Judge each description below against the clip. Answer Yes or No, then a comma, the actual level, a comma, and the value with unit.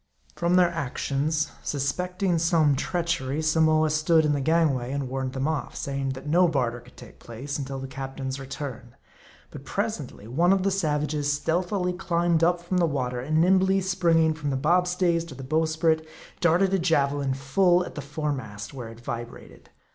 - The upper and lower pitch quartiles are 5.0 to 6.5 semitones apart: No, average, 4.1 semitones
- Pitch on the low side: No, medium, 155 Hz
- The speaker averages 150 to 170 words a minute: No, average, 180 wpm